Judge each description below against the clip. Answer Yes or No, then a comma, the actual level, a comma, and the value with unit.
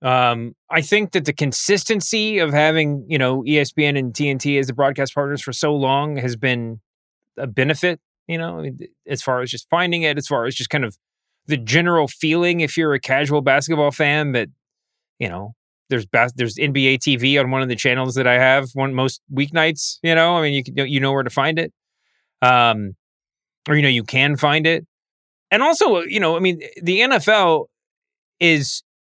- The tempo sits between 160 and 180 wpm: No, average, 195 wpm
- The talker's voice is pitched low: No, medium, 145 Hz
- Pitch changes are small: No, average, 3.8 semitones